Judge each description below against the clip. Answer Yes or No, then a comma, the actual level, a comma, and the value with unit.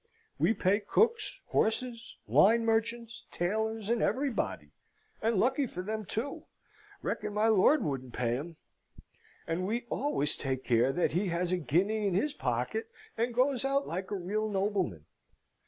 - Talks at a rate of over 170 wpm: No, average, 155 wpm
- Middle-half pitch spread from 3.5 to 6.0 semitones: Yes, average, 5.0 semitones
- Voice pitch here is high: Yes, high, 215 Hz